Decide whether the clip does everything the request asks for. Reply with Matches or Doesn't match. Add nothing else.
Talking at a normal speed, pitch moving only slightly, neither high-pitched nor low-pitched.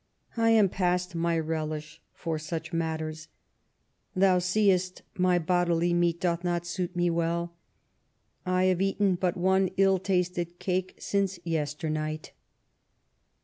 Doesn't match